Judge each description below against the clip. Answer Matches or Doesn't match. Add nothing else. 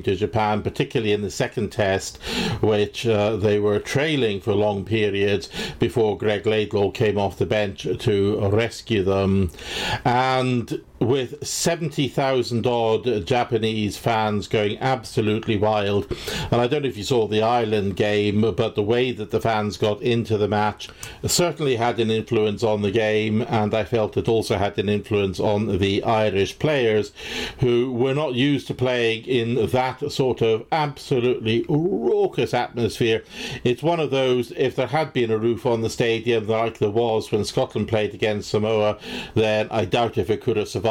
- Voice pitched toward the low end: Matches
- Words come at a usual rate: Matches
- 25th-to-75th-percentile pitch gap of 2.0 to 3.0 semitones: Matches